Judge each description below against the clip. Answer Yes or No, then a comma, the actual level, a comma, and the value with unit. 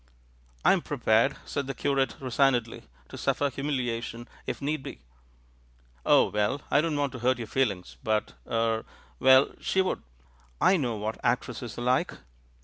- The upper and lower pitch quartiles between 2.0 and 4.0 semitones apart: Yes, average, 3.3 semitones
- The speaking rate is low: No, average, 170 wpm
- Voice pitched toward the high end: No, low, 125 Hz